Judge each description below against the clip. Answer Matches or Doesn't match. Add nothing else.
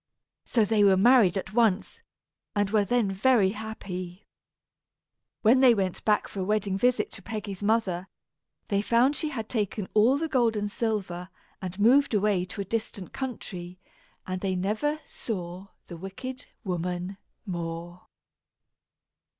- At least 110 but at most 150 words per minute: Matches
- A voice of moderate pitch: Doesn't match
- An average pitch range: Matches